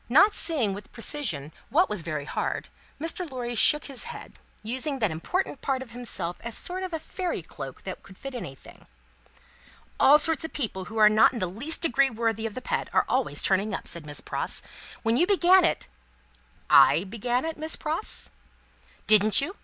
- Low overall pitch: No, high, 245 Hz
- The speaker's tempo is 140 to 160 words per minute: No, average, 190 wpm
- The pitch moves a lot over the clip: Yes, wide, 7.1 semitones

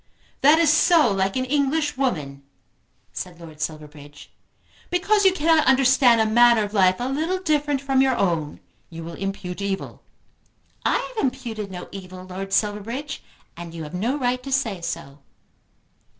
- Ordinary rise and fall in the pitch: No, wide, 7.3 semitones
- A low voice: No, high, 225 Hz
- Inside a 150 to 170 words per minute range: Yes, average, 160 wpm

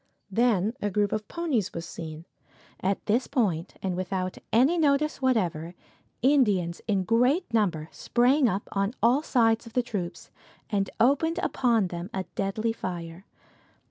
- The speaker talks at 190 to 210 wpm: No, average, 145 wpm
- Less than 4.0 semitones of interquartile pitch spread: No, average, 5.2 semitones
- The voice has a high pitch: Yes, high, 210 Hz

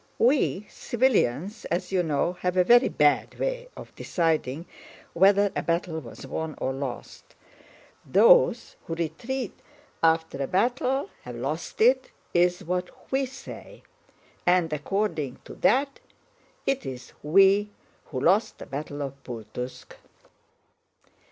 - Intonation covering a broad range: Yes, wide, 7.7 semitones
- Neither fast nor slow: No, slow, 125 wpm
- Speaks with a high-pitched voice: No, medium, 175 Hz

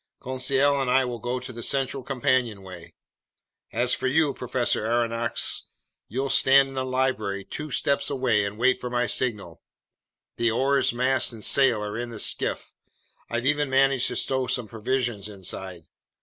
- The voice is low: Yes, low, 125 Hz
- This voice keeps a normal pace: Yes, average, 165 wpm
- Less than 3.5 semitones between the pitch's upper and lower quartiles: Yes, average, 2.8 semitones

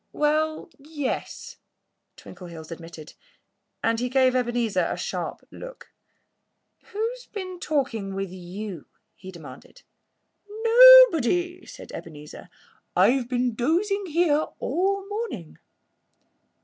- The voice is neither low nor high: No, very high, 265 Hz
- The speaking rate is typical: No, slow, 100 wpm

